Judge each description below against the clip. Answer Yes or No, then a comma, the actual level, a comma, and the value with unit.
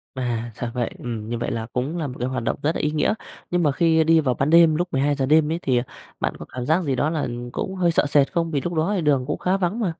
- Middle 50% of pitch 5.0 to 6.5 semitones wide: No, average, 4.6 semitones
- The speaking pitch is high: No, medium, 150 Hz